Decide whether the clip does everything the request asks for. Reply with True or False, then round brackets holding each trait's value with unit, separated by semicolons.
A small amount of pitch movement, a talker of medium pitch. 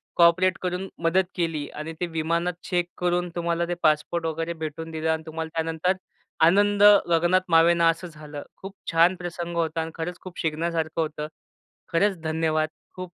True (1.6 semitones; 165 Hz)